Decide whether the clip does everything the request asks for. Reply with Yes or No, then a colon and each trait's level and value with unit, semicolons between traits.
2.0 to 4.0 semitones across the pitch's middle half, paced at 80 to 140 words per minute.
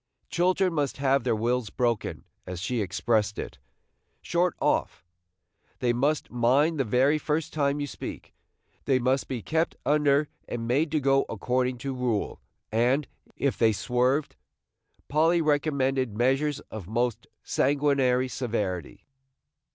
Yes: average, 3.5 semitones; slow, 135 wpm